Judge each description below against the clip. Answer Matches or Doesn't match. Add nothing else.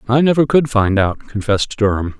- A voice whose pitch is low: Matches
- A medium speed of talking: Matches